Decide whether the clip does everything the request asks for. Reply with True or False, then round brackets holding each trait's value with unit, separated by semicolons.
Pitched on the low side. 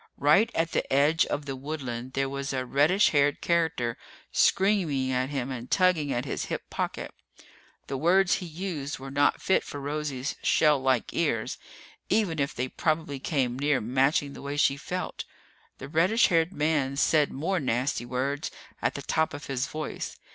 False (145 Hz)